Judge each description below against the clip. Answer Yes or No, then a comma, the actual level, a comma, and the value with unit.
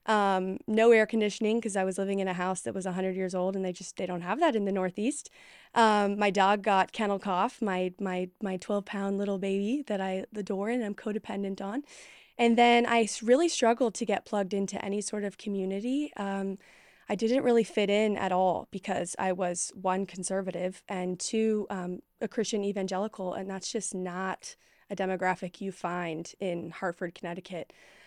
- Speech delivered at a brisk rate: No, average, 190 wpm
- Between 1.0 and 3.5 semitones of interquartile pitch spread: Yes, narrow, 2.5 semitones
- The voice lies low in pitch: No, high, 195 Hz